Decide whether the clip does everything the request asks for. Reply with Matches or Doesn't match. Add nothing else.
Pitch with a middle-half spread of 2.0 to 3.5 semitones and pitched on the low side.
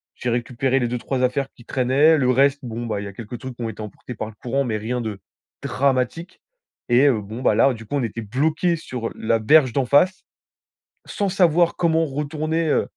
Doesn't match